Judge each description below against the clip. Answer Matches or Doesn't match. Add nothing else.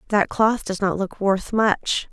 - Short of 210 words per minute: Matches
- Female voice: Matches